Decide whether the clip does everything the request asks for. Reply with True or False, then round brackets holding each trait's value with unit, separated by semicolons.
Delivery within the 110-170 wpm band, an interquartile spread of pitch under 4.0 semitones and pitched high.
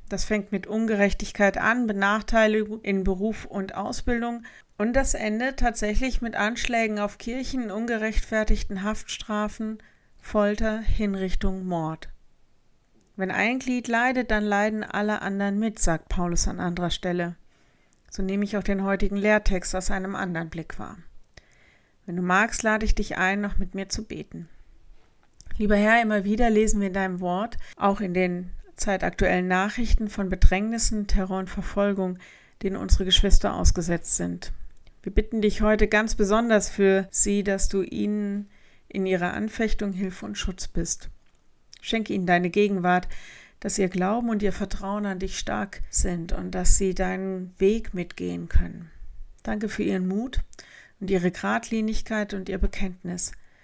True (150 wpm; 2.5 semitones; 200 Hz)